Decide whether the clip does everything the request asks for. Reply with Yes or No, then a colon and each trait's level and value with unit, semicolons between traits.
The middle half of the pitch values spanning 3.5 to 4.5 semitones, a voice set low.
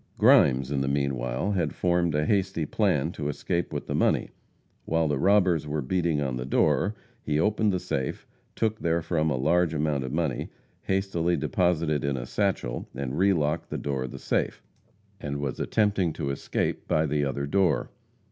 Yes: average, 4.1 semitones; very low, 75 Hz